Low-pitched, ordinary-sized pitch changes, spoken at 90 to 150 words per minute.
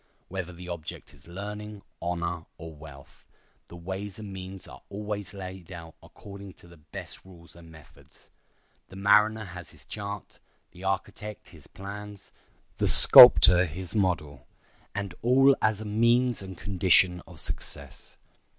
Yes: very low, 95 Hz; average, 3.1 semitones; average, 145 wpm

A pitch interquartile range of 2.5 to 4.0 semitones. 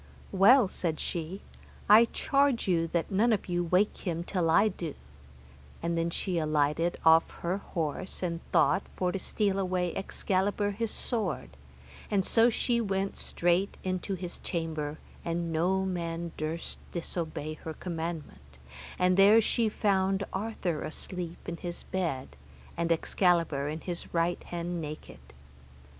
Yes: average, 2.8 semitones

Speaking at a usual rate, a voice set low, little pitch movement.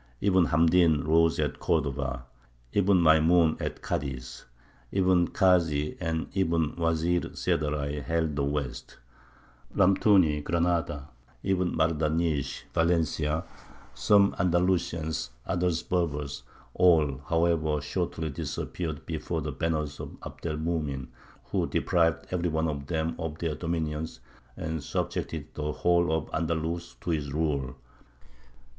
No: slow, 115 wpm; very low, 80 Hz; narrow, 2.3 semitones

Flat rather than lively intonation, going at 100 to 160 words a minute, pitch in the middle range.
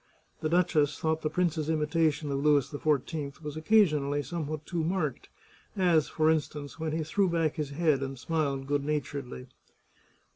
Yes: narrow, 2.1 semitones; average, 155 wpm; medium, 155 Hz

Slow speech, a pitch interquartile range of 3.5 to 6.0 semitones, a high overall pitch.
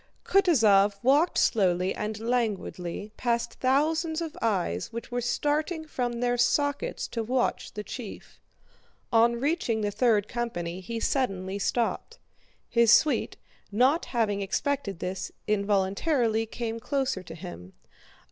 Yes: slow, 125 wpm; average, 4.8 semitones; high, 230 Hz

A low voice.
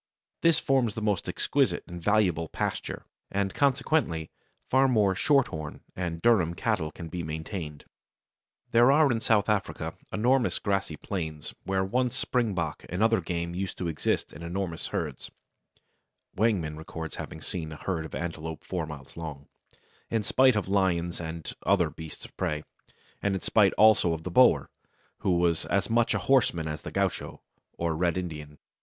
Yes: very low, 90 Hz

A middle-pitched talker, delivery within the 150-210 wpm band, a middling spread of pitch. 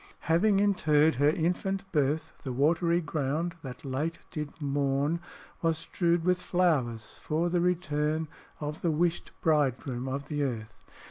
No: medium, 155 Hz; average, 140 wpm; average, 3.3 semitones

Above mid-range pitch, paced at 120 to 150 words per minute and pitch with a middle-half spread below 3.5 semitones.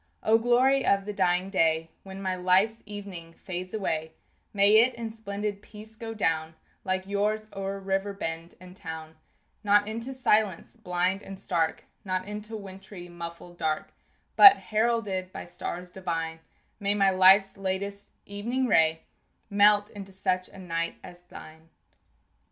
Yes: high, 195 Hz; average, 145 wpm; average, 2.9 semitones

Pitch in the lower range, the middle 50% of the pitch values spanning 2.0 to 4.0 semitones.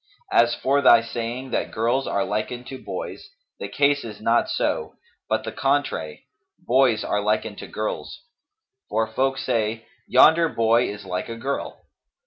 Yes: low, 115 Hz; average, 3.3 semitones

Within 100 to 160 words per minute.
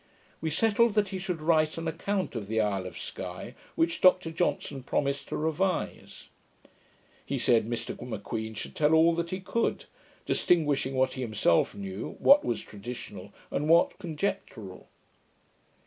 Yes: average, 150 wpm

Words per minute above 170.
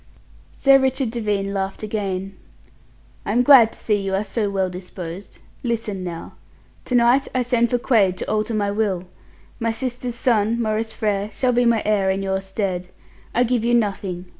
Yes: average, 180 wpm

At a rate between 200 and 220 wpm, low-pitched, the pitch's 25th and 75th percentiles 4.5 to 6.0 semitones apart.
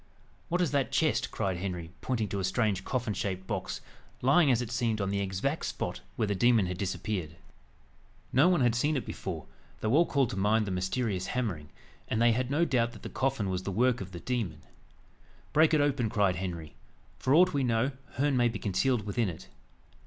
Yes: fast, 205 wpm; low, 115 Hz; average, 5.3 semitones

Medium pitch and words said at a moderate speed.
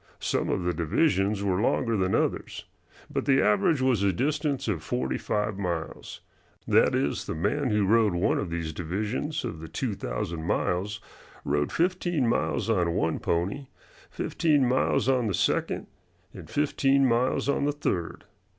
No: low, 105 Hz; average, 160 wpm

